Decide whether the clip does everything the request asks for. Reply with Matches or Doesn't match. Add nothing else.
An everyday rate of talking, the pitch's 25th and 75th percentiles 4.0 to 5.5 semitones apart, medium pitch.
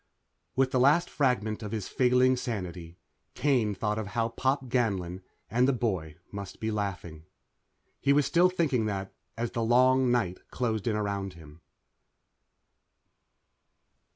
Doesn't match